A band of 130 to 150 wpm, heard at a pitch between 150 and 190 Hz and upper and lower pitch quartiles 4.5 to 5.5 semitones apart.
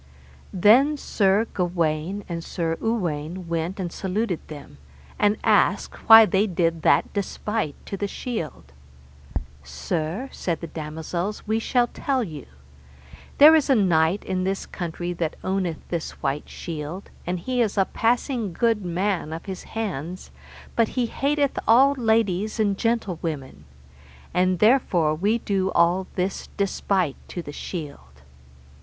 Yes: average, 140 wpm; medium, 185 Hz; average, 4.9 semitones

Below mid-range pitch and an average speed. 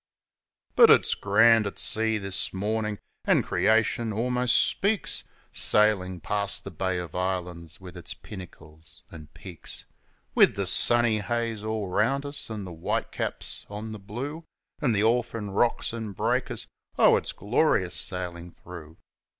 Yes: low, 105 Hz; average, 145 wpm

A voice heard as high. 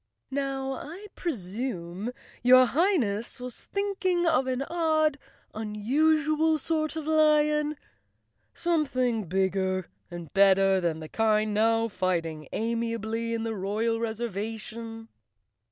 Yes: high, 230 Hz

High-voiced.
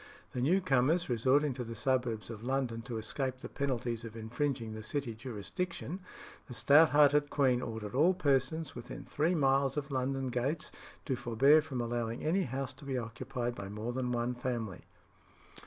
No: low, 130 Hz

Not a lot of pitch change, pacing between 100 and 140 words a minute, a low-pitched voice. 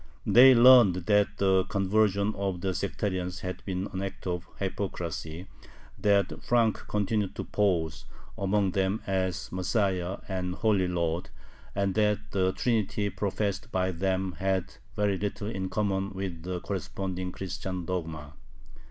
Yes: narrow, 1.9 semitones; slow, 135 wpm; very low, 95 Hz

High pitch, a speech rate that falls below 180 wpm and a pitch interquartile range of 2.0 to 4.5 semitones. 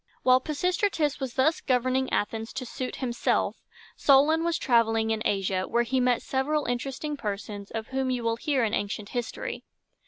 Yes: very high, 255 Hz; average, 165 wpm; average, 3.5 semitones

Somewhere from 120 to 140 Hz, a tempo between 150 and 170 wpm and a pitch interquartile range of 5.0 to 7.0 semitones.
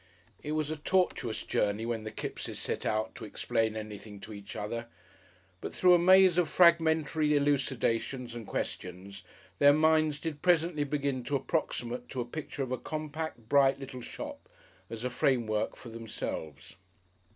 Yes: low, 135 Hz; average, 160 wpm; wide, 5.6 semitones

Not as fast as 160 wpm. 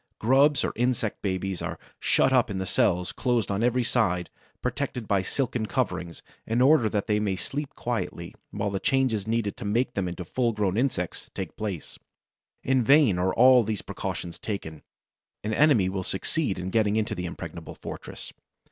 No: average, 175 wpm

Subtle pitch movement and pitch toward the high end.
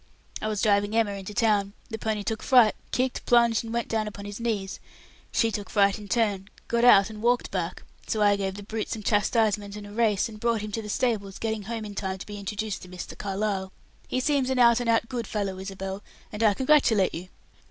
Yes: narrow, 2.3 semitones; high, 210 Hz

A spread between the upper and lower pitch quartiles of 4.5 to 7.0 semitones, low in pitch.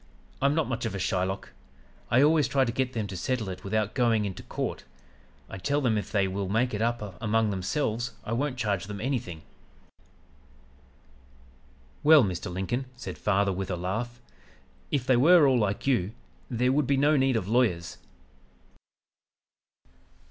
Yes: average, 4.9 semitones; low, 115 Hz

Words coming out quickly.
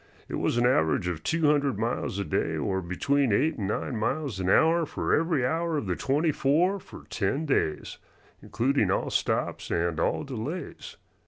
No: average, 180 wpm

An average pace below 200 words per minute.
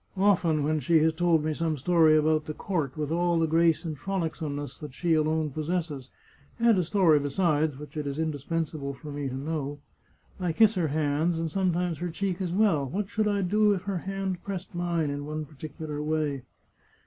No: fast, 205 wpm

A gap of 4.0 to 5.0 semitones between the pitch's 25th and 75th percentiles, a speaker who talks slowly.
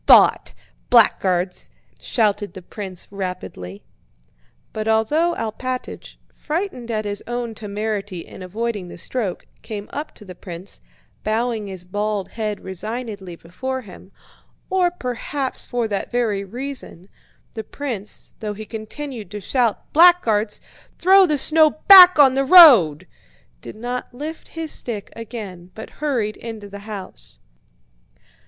Yes: average, 4.5 semitones; slow, 130 wpm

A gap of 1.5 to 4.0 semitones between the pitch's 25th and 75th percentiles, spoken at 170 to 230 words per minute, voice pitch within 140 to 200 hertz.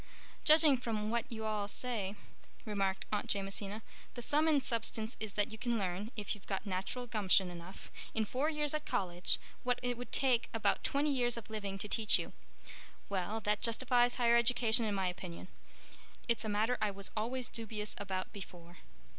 No: average, 3.5 semitones; average, 175 wpm; high, 220 Hz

